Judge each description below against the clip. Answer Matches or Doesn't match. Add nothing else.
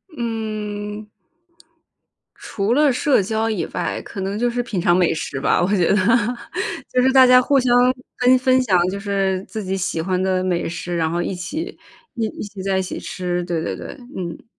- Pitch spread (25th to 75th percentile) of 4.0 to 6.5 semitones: Matches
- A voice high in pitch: Matches